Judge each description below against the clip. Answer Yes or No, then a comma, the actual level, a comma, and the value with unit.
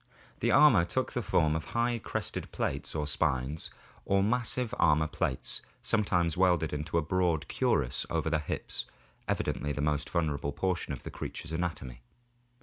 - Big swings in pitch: No, average, 3.8 semitones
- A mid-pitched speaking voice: No, very low, 80 Hz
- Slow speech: No, average, 160 wpm